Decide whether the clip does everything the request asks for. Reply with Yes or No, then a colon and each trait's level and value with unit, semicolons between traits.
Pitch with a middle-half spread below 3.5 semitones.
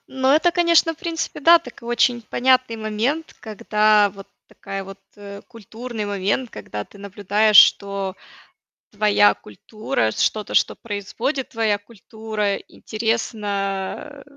No: average, 3.8 semitones